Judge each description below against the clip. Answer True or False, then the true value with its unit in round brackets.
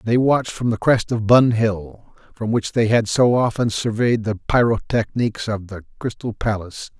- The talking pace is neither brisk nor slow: True (180 wpm)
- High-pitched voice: False (110 Hz)